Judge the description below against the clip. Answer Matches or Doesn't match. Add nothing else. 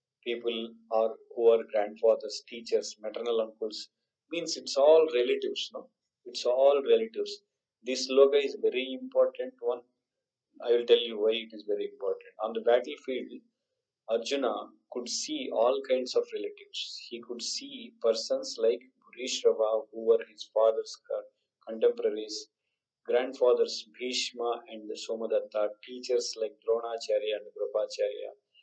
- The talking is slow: Matches